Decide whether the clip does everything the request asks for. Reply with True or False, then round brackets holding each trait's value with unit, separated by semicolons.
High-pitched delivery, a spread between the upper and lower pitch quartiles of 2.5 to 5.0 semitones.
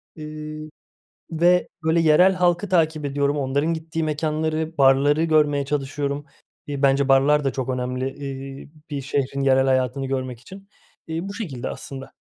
False (145 Hz; 2.8 semitones)